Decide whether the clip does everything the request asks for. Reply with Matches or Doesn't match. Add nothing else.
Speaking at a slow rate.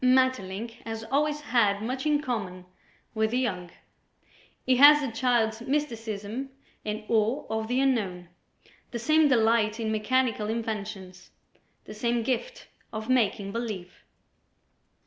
Matches